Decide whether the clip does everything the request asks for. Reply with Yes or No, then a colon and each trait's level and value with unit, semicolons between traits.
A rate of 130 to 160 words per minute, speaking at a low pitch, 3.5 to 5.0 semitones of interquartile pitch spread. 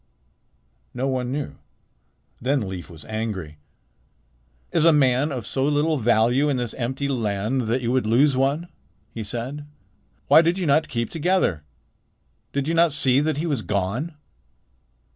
Yes: average, 155 wpm; low, 130 Hz; average, 4.5 semitones